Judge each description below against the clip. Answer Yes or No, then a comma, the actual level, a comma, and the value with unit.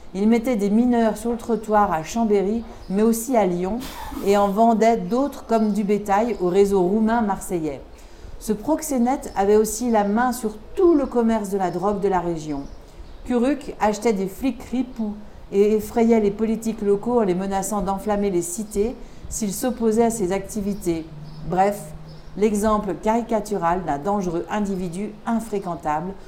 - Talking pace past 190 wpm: No, average, 155 wpm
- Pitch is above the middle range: Yes, high, 210 Hz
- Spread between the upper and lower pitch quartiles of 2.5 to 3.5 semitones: Yes, average, 2.9 semitones